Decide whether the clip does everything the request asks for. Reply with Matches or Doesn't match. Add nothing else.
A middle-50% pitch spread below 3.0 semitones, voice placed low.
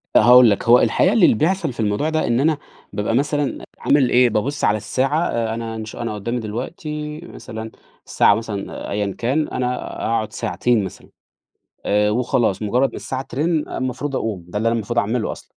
Doesn't match